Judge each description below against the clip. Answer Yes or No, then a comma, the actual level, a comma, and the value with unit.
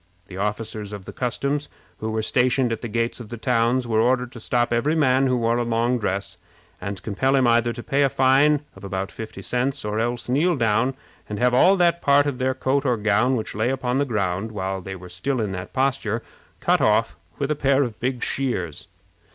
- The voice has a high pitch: No, low, 120 Hz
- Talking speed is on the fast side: Yes, fast, 215 wpm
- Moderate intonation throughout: Yes, average, 3.7 semitones